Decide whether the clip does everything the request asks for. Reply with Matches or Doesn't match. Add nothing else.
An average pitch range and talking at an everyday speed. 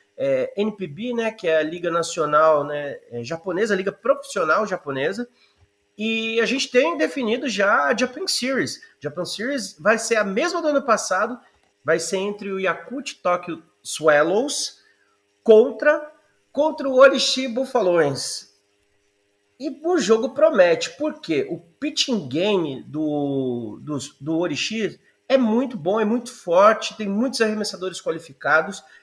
Doesn't match